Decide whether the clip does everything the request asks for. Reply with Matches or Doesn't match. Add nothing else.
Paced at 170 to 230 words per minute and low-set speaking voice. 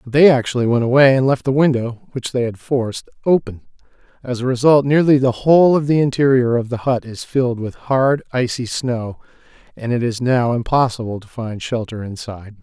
Matches